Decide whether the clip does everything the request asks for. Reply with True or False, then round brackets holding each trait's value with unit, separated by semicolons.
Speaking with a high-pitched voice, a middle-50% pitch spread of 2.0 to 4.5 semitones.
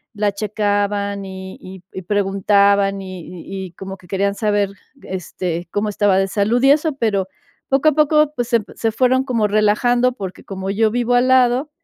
True (205 Hz; 4.0 semitones)